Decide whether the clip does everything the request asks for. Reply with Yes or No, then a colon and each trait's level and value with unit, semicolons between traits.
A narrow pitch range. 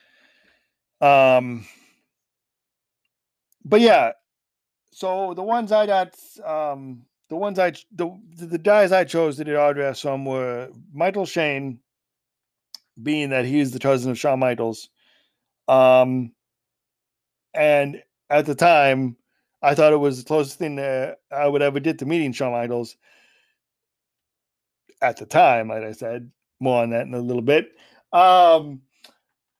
No: average, 4.6 semitones